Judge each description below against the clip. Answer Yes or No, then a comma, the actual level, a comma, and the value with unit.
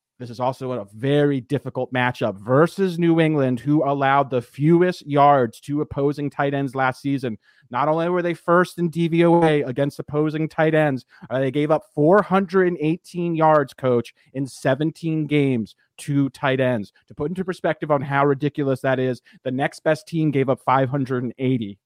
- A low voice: No, medium, 145 Hz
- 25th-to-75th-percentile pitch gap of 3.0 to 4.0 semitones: Yes, average, 3.4 semitones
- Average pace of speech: Yes, average, 165 wpm